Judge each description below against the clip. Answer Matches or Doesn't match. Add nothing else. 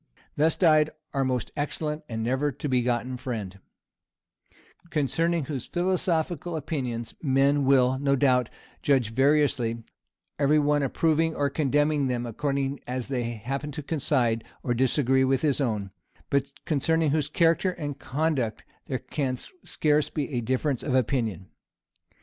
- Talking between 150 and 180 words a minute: Doesn't match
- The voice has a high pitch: Doesn't match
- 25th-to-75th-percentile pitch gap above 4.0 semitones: Doesn't match